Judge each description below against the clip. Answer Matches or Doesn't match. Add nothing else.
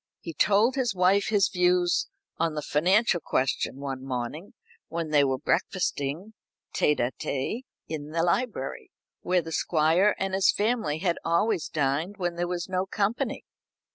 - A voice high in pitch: Doesn't match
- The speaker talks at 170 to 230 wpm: Doesn't match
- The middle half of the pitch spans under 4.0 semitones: Doesn't match